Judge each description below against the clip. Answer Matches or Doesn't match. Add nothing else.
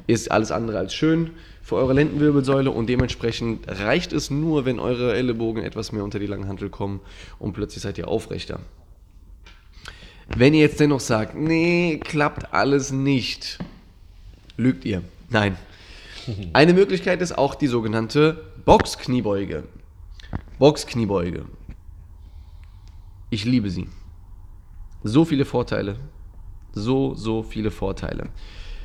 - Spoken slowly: Matches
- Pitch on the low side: Matches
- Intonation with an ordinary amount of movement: Doesn't match